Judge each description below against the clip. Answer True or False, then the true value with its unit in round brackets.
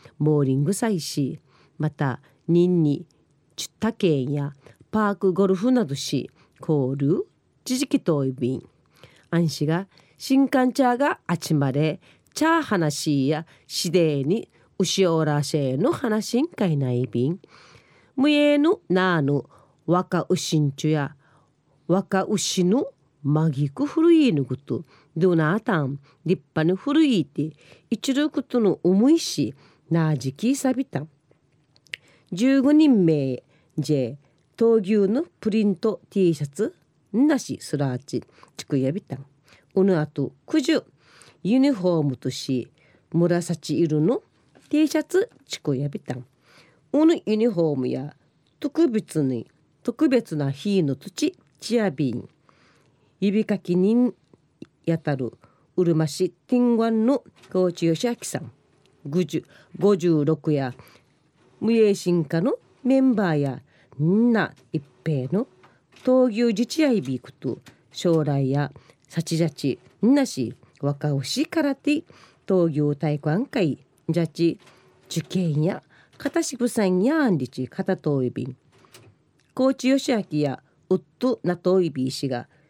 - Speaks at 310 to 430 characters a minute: False (225 characters per minute)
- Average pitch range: False (7.2 semitones)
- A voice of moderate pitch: True (165 Hz)